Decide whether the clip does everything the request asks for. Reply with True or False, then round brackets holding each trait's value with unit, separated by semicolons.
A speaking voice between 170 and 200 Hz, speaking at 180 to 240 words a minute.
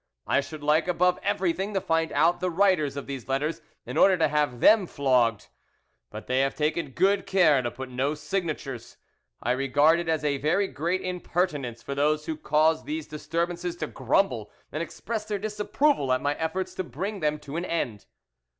False (155 Hz; 185 wpm)